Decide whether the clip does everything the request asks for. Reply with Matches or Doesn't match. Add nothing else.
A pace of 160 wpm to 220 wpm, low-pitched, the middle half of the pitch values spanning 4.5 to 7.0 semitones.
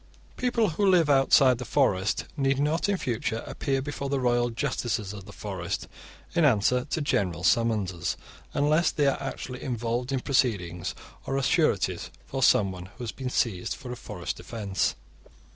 Matches